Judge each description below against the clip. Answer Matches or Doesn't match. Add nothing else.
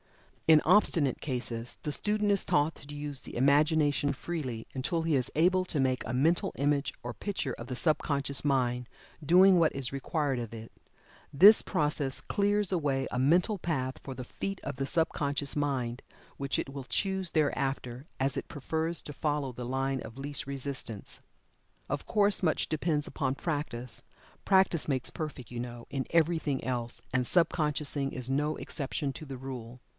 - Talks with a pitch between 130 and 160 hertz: Matches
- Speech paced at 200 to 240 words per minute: Doesn't match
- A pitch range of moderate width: Matches